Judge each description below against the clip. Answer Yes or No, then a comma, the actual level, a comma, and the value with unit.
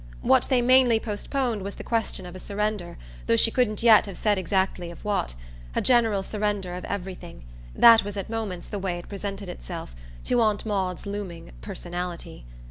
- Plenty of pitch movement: No, average, 3.4 semitones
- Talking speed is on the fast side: No, average, 180 wpm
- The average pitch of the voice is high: Yes, high, 200 Hz